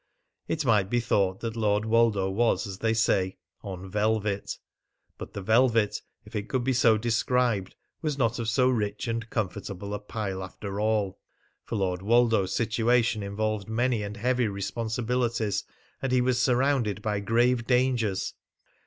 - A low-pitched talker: Yes, low, 110 Hz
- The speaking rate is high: No, average, 155 wpm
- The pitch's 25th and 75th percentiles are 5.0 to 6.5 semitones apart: No, average, 3.0 semitones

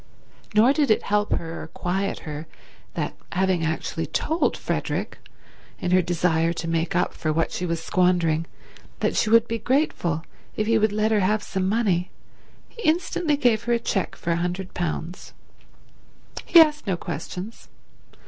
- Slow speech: No, average, 160 wpm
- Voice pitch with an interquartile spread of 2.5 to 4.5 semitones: No, average, 4.9 semitones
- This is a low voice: No, medium, 185 Hz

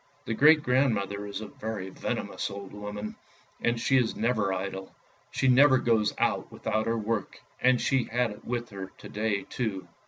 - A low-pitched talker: Yes, low, 110 Hz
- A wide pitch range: No, average, 3.4 semitones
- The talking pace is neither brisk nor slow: Yes, average, 180 wpm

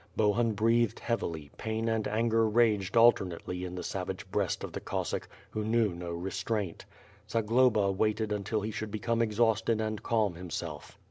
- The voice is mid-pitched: No, low, 110 Hz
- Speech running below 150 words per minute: No, average, 155 wpm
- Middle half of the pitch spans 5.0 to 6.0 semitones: No, narrow, 2.6 semitones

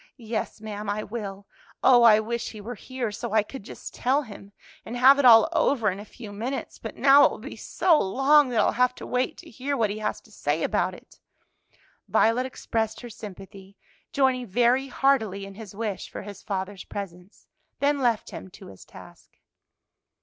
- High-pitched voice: Yes, high, 225 Hz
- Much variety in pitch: No, average, 3.9 semitones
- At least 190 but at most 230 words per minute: Yes, average, 195 wpm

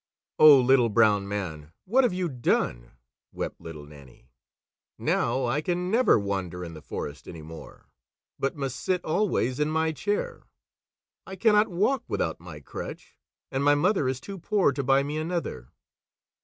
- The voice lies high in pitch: No, low, 135 Hz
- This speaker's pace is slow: No, average, 160 wpm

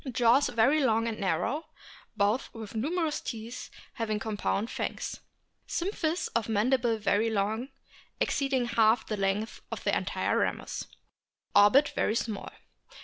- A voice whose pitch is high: Yes, high, 225 Hz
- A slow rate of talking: Yes, slow, 130 wpm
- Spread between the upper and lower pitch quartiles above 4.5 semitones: No, average, 3.4 semitones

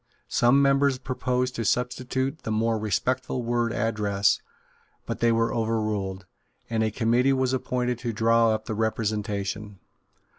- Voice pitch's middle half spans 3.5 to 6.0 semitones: No, average, 2.7 semitones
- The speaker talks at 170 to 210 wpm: No, average, 140 wpm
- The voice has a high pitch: No, low, 115 Hz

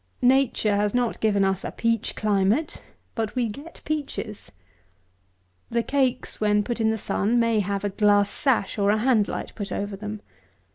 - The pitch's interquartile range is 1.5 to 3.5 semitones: Yes, average, 2.9 semitones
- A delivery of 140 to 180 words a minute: Yes, average, 175 wpm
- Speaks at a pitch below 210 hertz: No, high, 215 Hz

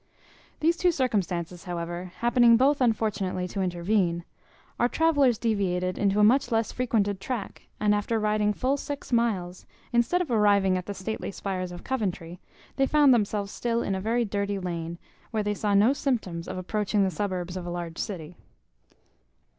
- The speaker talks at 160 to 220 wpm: Yes, average, 170 wpm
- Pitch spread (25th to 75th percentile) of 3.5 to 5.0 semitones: Yes, average, 4.4 semitones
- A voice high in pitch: Yes, high, 205 Hz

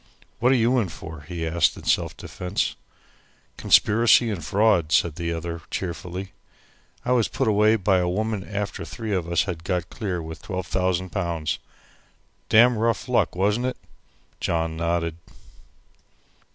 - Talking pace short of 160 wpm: Yes, average, 150 wpm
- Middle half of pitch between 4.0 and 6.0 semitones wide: Yes, average, 4.4 semitones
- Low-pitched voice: Yes, very low, 95 Hz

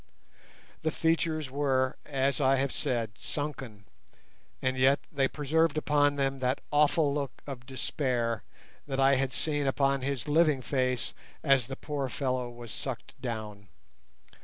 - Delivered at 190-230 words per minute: No, average, 140 wpm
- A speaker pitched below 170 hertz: Yes, low, 135 Hz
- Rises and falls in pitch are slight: Yes, narrow, 2.2 semitones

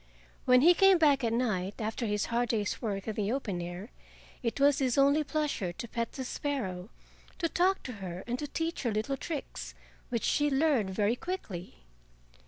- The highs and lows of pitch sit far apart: Yes, wide, 5.7 semitones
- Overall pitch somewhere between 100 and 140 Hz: No, high, 240 Hz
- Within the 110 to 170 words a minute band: No, average, 190 wpm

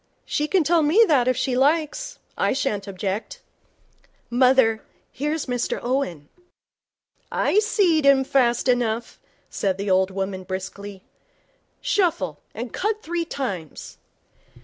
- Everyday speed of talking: No, slow, 125 wpm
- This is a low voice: No, very high, 255 Hz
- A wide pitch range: Yes, wide, 7.7 semitones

